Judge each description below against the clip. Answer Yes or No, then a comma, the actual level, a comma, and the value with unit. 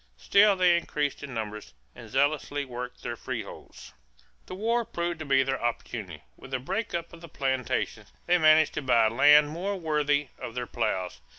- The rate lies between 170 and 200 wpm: Yes, average, 180 wpm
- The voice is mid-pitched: Yes, medium, 145 Hz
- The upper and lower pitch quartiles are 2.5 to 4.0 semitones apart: No, average, 5.2 semitones